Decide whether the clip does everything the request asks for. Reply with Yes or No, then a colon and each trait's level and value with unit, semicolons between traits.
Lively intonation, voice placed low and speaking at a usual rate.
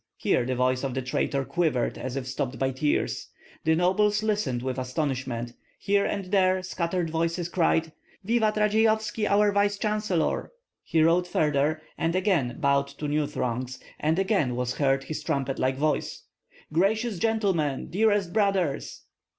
No: wide, 6.8 semitones; medium, 165 Hz; average, 150 wpm